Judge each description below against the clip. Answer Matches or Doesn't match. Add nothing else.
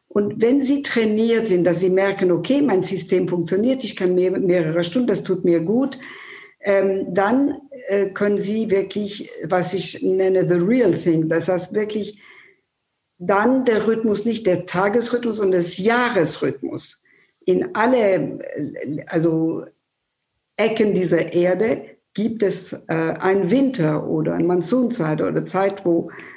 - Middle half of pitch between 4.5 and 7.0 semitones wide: Doesn't match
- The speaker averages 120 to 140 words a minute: Matches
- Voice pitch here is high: Matches